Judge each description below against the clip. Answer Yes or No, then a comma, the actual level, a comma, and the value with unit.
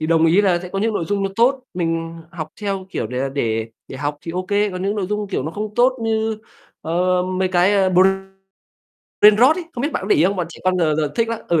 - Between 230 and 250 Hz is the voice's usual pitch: No, medium, 185 Hz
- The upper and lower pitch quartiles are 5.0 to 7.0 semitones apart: No, average, 4.1 semitones